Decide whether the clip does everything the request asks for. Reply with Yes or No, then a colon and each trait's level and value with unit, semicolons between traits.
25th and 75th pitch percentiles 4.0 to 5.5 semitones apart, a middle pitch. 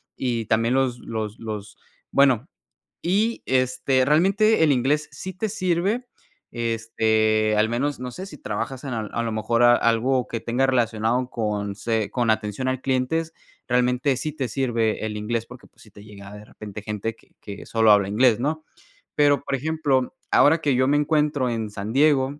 No: average, 4.4 semitones; low, 125 Hz